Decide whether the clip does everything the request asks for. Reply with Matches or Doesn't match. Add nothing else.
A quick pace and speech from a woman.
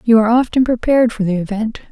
Matches